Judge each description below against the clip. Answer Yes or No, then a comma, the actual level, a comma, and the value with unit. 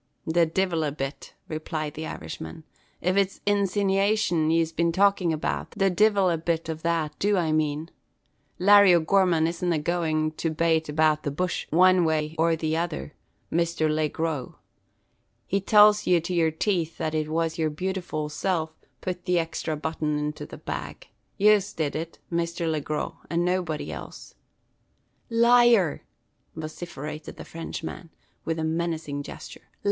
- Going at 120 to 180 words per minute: Yes, average, 150 wpm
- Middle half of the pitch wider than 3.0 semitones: No, narrow, 2.6 semitones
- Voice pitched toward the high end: No, medium, 165 Hz